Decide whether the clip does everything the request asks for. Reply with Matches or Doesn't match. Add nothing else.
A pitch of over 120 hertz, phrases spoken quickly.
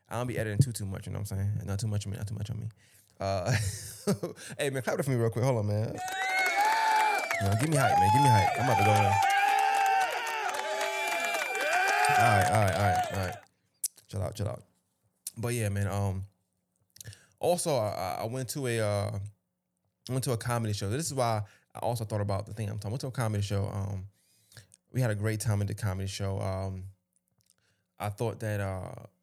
Doesn't match